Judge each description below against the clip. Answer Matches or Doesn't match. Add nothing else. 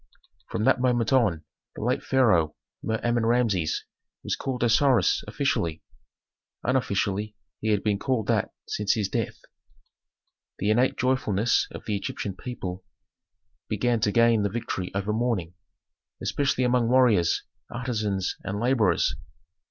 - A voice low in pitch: Matches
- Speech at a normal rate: Doesn't match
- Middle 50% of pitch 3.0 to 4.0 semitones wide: Matches